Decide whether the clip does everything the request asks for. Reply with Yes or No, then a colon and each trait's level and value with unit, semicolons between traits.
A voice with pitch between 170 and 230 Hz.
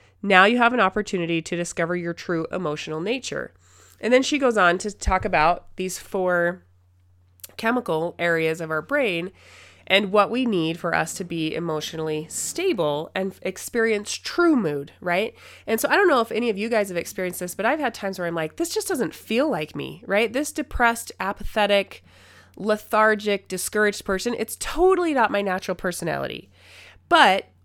Yes: high, 190 Hz